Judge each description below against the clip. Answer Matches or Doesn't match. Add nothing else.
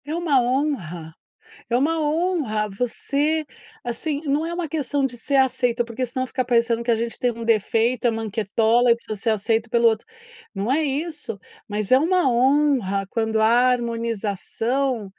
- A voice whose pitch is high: Matches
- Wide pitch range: Doesn't match